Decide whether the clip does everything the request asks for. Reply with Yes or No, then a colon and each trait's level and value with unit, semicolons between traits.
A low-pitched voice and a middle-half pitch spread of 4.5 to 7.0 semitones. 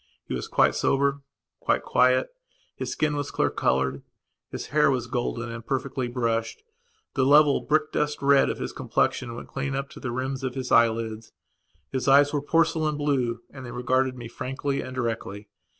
No: low, 130 Hz; average, 3.0 semitones